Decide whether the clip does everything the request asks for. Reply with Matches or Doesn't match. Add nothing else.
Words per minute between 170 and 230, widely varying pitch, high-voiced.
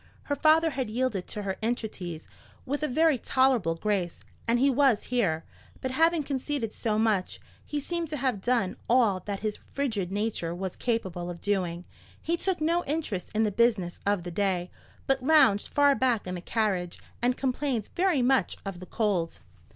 Matches